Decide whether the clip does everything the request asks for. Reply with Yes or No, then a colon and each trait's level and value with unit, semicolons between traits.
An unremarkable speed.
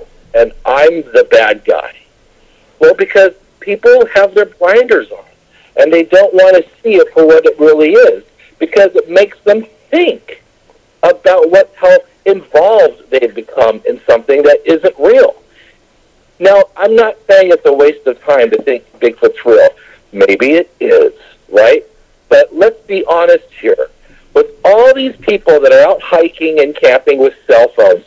Yes: average, 160 wpm